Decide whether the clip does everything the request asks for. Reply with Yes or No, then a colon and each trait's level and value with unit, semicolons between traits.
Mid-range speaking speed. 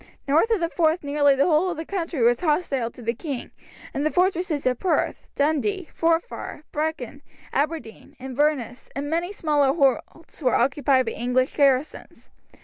Yes: average, 160 wpm